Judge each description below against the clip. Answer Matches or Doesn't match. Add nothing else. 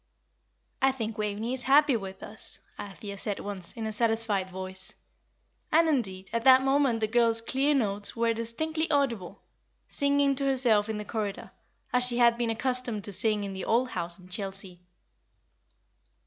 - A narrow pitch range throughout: Doesn't match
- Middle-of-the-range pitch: Doesn't match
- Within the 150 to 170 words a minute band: Matches